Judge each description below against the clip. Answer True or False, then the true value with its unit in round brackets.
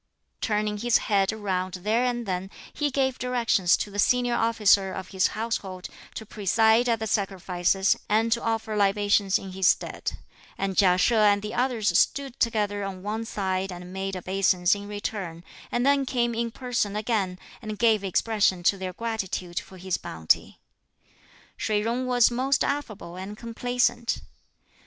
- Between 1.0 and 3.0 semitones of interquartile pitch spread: False (3.4 semitones)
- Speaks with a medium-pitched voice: False (210 Hz)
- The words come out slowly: False (160 wpm)